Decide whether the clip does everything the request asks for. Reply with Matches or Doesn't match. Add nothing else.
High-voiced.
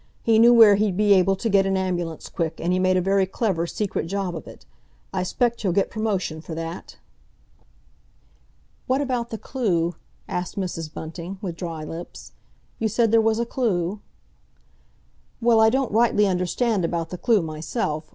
Matches